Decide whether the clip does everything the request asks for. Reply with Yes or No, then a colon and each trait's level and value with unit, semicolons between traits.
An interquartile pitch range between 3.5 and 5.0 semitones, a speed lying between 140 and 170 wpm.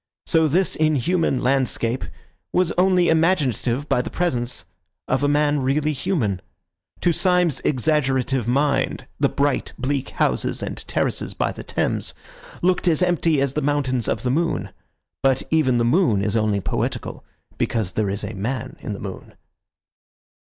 Yes: average, 4.6 semitones; average, 155 wpm